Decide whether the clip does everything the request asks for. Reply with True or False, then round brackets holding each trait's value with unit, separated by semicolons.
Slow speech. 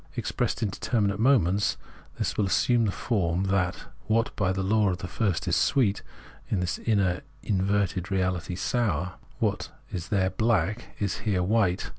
False (165 wpm)